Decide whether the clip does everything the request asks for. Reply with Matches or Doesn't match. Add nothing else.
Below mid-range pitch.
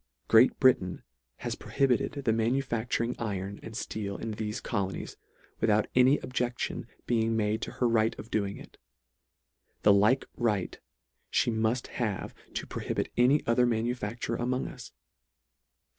Matches